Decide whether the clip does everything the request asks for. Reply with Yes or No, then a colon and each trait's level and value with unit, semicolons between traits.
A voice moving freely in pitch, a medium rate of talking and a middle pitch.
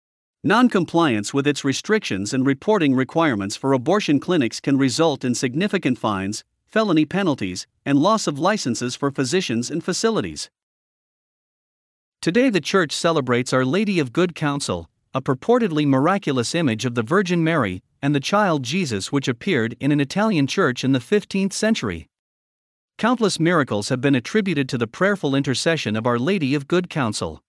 Yes: wide, 6.0 semitones; average, 155 wpm; medium, 145 Hz